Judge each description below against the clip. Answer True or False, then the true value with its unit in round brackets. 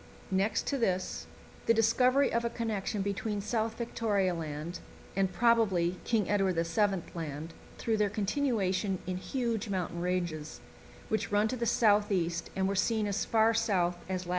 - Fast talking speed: False (165 wpm)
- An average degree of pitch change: True (3.7 semitones)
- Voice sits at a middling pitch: False (200 Hz)